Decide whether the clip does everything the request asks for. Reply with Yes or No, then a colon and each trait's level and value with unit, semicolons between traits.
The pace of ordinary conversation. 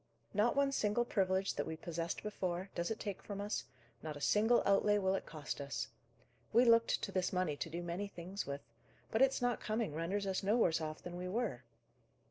No: fast, 210 wpm